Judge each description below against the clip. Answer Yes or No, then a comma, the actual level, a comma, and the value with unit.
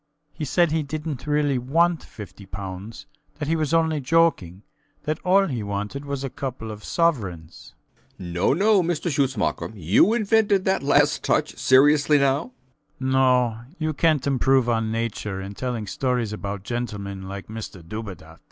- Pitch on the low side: Yes, low, 130 Hz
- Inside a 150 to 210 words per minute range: Yes, average, 160 wpm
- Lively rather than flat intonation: Yes, wide, 6.9 semitones